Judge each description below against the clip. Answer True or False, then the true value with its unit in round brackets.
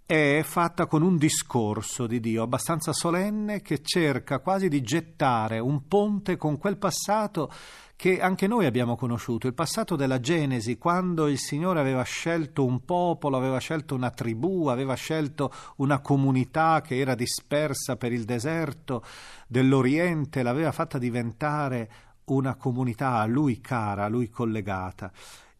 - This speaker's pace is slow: False (145 wpm)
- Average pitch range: True (5.0 semitones)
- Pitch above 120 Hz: True (140 Hz)